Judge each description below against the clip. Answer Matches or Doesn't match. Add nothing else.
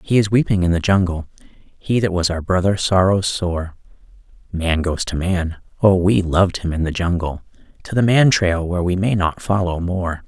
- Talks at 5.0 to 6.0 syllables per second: Doesn't match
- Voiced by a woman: Doesn't match